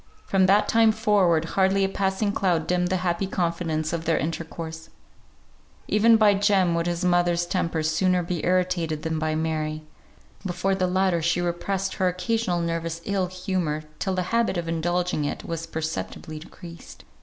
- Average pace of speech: Yes, average, 165 wpm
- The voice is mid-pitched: Yes, medium, 175 Hz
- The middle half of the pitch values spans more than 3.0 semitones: No, narrow, 2.6 semitones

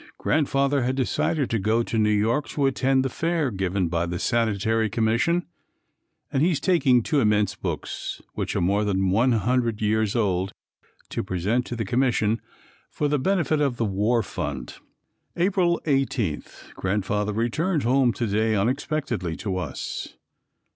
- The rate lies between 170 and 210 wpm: No, average, 155 wpm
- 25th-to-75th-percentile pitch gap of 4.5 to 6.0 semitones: Yes, average, 4.8 semitones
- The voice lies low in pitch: Yes, low, 115 Hz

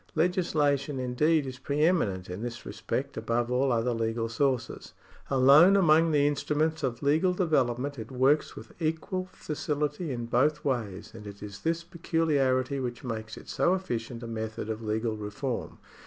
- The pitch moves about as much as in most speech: Yes, average, 5.0 semitones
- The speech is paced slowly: No, average, 160 wpm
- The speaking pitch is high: No, low, 135 Hz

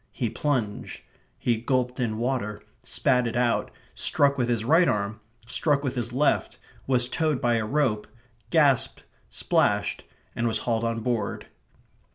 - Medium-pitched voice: No, low, 120 Hz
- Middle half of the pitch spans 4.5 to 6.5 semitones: No, average, 3.0 semitones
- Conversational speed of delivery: Yes, average, 150 wpm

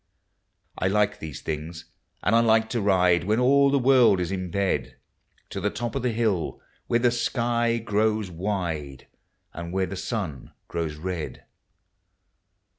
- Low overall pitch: Yes, low, 100 Hz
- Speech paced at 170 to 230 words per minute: No, average, 155 wpm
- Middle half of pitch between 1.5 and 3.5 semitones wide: No, average, 5.2 semitones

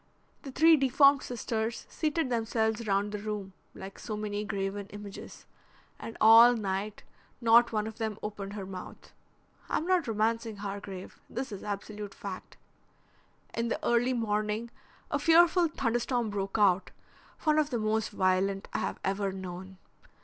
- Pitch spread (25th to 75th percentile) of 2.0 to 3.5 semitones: Yes, average, 3.0 semitones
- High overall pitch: Yes, high, 215 Hz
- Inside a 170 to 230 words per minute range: No, average, 150 wpm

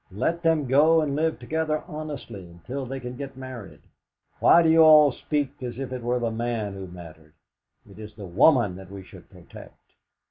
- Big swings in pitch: Yes, wide, 6.7 semitones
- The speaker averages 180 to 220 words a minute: Yes, average, 190 wpm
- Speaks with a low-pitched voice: Yes, low, 130 Hz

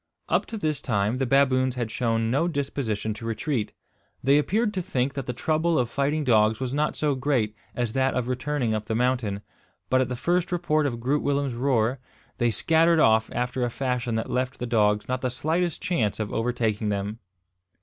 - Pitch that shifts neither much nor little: Yes, average, 4.1 semitones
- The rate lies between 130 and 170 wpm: No, average, 200 wpm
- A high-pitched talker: No, low, 125 Hz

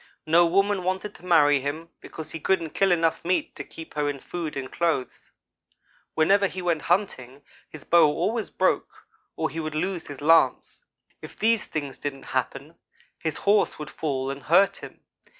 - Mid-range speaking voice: Yes, medium, 165 Hz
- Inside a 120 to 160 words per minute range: No, average, 175 wpm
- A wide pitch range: No, average, 4.0 semitones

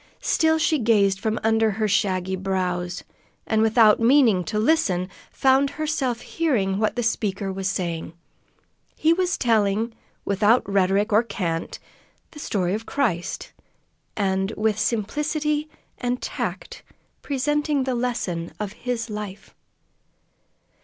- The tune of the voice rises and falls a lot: No, average, 5.0 semitones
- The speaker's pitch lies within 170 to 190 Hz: No, high, 220 Hz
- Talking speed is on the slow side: Yes, slow, 125 wpm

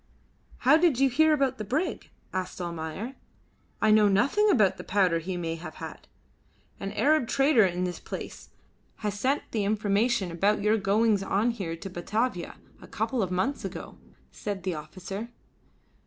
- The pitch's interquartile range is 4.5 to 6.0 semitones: Yes, average, 4.9 semitones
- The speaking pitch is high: Yes, high, 205 Hz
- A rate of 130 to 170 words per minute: Yes, average, 165 wpm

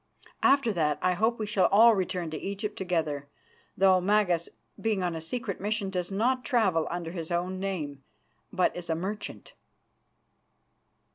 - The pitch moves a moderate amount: Yes, average, 3.7 semitones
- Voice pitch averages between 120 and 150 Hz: No, medium, 185 Hz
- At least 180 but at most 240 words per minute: No, average, 155 wpm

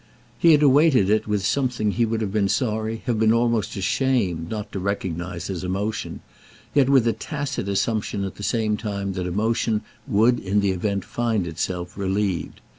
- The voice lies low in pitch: Yes, low, 105 Hz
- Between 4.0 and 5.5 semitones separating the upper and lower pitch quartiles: No, average, 3.2 semitones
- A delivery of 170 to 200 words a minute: Yes, average, 180 wpm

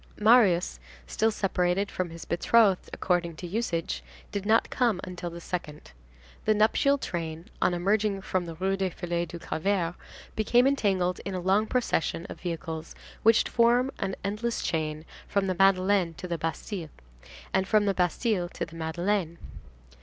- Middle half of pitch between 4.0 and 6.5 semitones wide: No, average, 3.6 semitones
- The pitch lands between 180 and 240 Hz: Yes, medium, 185 Hz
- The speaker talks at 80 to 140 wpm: No, average, 160 wpm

